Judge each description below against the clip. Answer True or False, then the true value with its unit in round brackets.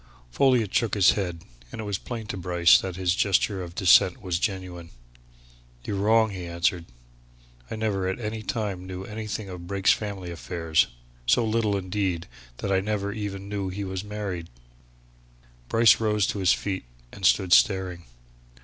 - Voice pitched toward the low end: True (95 Hz)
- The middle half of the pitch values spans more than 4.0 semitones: False (2.6 semitones)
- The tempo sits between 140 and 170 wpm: True (165 wpm)